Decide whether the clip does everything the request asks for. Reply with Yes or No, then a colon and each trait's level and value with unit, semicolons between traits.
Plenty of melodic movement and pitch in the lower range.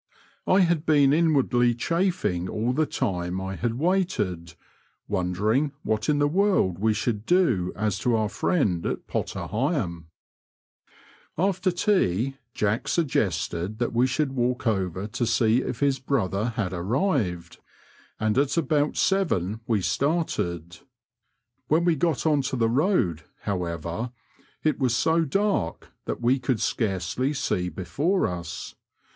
Yes: wide, 8.3 semitones; low, 120 Hz